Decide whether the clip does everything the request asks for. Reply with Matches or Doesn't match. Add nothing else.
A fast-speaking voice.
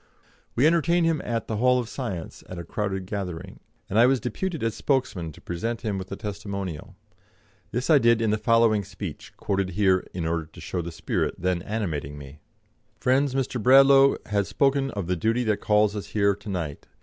Doesn't match